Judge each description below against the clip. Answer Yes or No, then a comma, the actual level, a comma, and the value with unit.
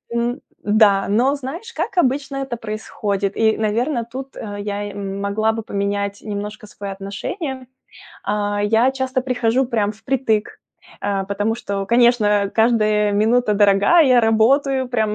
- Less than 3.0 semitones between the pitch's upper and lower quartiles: No, average, 3.6 semitones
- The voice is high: Yes, high, 220 Hz